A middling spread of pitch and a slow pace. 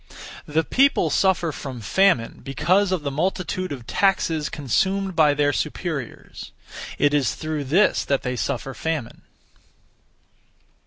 Yes: average, 5.0 semitones; slow, 125 wpm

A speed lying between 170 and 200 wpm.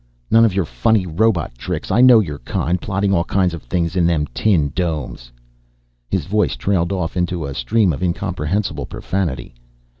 Yes: average, 175 wpm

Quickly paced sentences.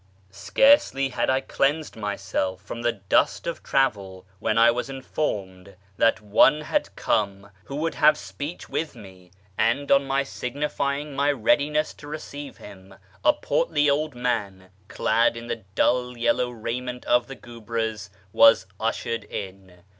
No: average, 145 wpm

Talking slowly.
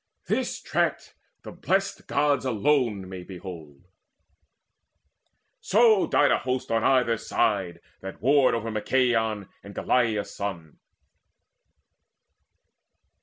Yes: slow, 100 wpm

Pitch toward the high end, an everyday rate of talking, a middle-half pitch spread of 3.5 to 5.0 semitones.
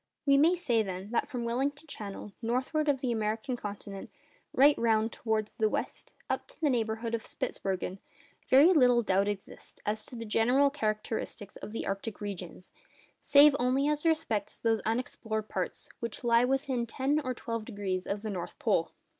Yes: high, 230 Hz; average, 170 wpm; average, 4.1 semitones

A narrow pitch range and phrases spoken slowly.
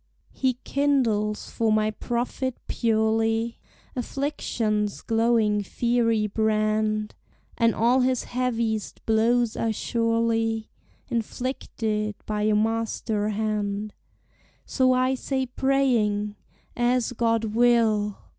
Yes: narrow, 2.2 semitones; slow, 95 wpm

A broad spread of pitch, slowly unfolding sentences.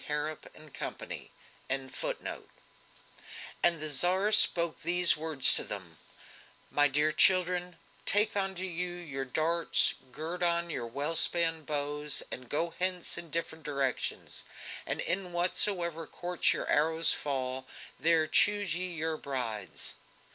No: average, 3.3 semitones; slow, 125 wpm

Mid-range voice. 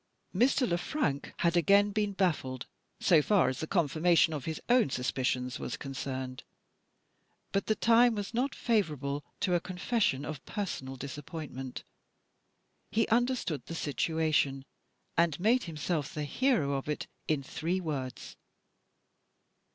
Yes: medium, 160 Hz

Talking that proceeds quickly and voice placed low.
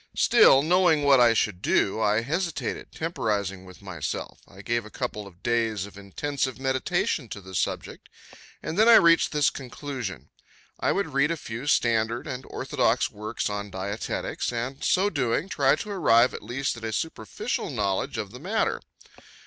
No: average, 170 wpm; low, 120 Hz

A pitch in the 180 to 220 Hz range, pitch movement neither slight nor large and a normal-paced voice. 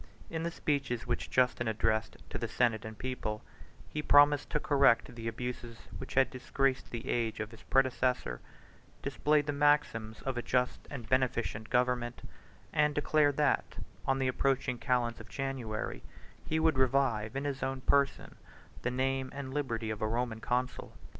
No: low, 130 Hz; average, 3.0 semitones; average, 165 wpm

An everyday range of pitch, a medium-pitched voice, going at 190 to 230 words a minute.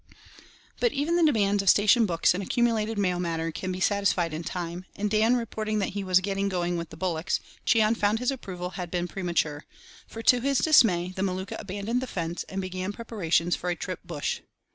No: average, 3.7 semitones; high, 195 Hz; fast, 205 wpm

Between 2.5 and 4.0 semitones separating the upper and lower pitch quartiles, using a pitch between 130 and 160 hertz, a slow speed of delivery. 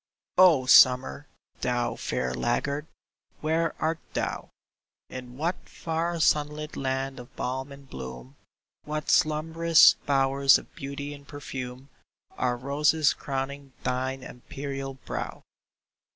Yes: average, 2.8 semitones; medium, 140 Hz; slow, 115 wpm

